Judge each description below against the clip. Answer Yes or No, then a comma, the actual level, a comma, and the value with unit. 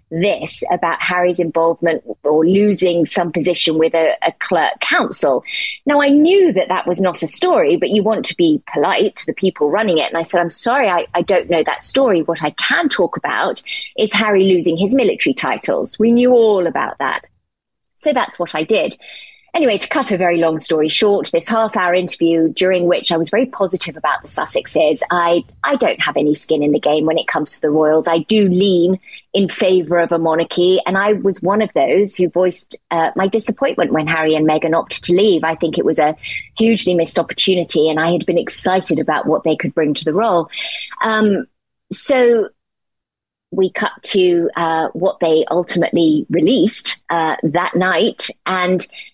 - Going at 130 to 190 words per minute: No, average, 200 wpm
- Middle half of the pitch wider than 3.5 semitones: Yes, average, 4.3 semitones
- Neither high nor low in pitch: Yes, medium, 180 Hz